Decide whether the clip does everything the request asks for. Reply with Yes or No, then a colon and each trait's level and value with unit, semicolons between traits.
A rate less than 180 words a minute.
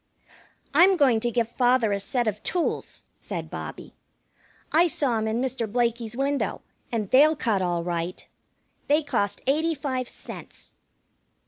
Yes: average, 145 wpm